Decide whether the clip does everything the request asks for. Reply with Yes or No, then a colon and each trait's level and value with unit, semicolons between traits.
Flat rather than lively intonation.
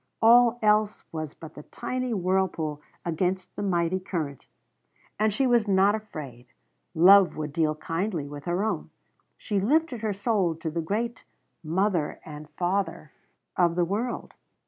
No: average, 4.9 semitones